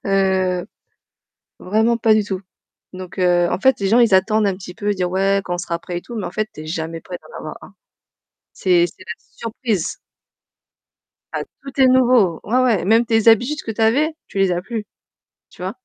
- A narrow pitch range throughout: No, average, 4.1 semitones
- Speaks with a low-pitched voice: No, high, 200 Hz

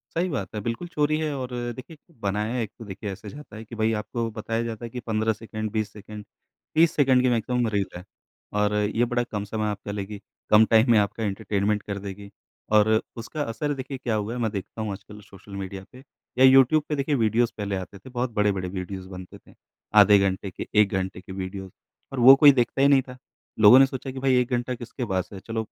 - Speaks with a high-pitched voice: No, low, 110 Hz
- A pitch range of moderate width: Yes, average, 3.8 semitones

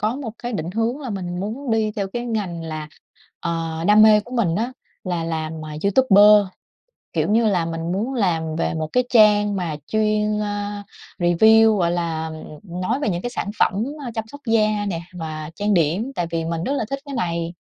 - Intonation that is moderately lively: Yes, average, 4.9 semitones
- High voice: Yes, high, 205 Hz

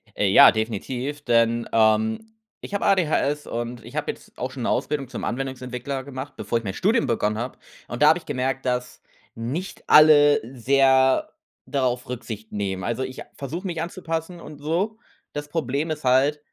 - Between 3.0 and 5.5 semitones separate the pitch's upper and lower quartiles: Yes, average, 4.1 semitones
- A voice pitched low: Yes, low, 130 Hz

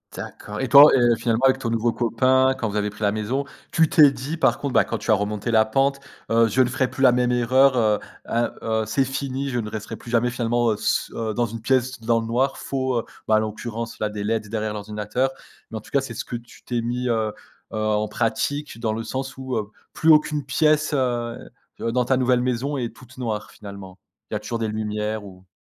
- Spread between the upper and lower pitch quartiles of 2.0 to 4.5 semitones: Yes, average, 3.2 semitones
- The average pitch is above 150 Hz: No, low, 120 Hz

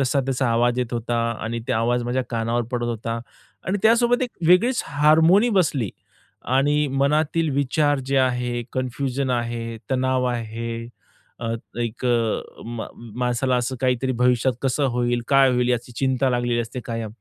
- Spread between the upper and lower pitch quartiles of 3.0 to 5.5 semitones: No, narrow, 2.6 semitones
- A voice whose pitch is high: No, low, 125 Hz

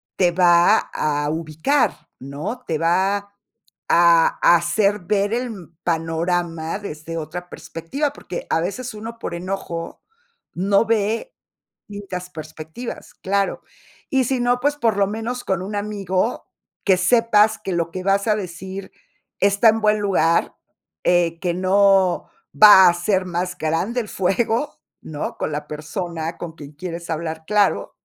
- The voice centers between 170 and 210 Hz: Yes, medium, 185 Hz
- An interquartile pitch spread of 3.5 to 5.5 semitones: Yes, average, 3.9 semitones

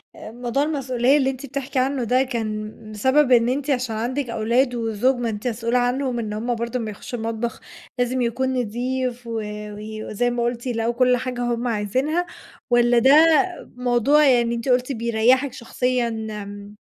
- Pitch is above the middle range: Yes, high, 245 Hz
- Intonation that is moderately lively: No, narrow, 2.1 semitones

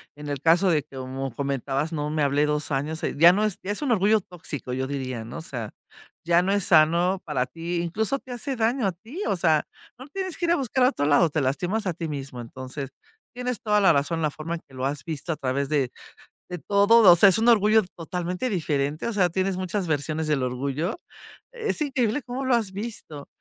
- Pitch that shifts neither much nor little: No, wide, 6.6 semitones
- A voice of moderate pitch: Yes, medium, 170 Hz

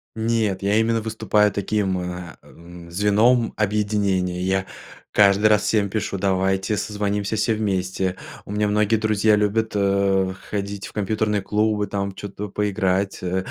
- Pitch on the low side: Yes, low, 100 Hz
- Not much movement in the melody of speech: Yes, narrow, 1.7 semitones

